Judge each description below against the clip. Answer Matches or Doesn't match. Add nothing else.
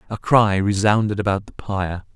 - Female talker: Doesn't match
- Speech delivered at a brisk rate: Doesn't match